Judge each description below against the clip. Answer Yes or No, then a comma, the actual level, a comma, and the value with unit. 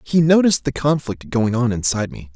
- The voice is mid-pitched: No, low, 125 Hz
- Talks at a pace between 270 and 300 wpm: No, fast, 205 wpm